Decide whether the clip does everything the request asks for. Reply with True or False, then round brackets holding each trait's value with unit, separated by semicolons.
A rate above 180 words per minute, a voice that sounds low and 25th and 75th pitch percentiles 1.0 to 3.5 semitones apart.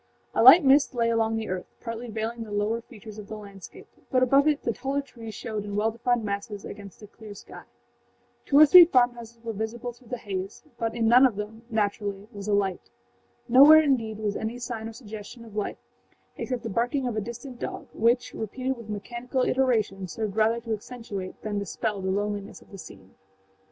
False (200 wpm; 225 Hz; 2.9 semitones)